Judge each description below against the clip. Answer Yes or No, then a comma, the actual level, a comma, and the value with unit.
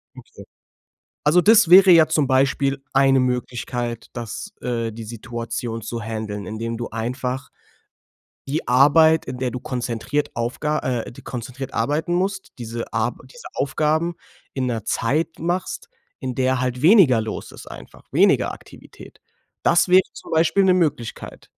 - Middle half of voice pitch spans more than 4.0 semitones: Yes, average, 5.2 semitones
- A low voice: Yes, low, 130 Hz